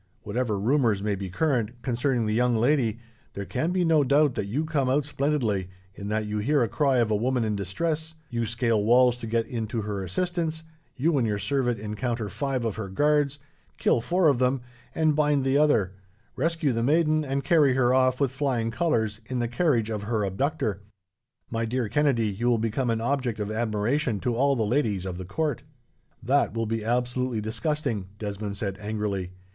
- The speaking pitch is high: No, low, 120 Hz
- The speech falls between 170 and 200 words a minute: Yes, average, 195 wpm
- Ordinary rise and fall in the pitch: Yes, average, 4.7 semitones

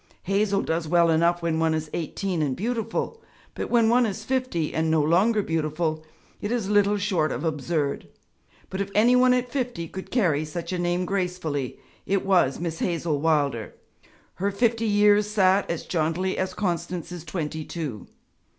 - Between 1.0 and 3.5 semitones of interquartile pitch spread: No, average, 4.4 semitones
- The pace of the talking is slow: No, average, 170 wpm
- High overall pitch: No, medium, 175 Hz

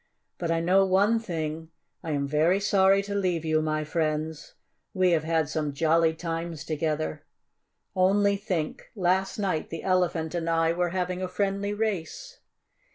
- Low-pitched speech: No, medium, 170 Hz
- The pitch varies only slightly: No, average, 3.3 semitones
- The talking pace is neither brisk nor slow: Yes, average, 160 wpm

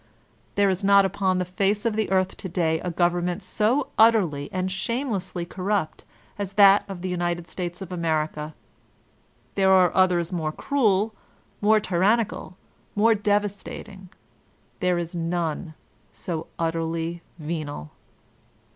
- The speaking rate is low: Yes, slow, 130 wpm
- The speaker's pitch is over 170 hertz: Yes, medium, 185 Hz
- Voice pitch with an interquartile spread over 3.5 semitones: No, average, 2.9 semitones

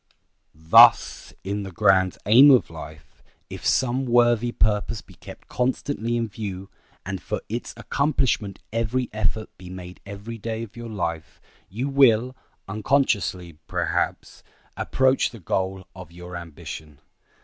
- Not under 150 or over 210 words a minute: No, slow, 135 wpm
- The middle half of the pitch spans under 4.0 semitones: No, average, 4.4 semitones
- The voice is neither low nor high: No, low, 105 Hz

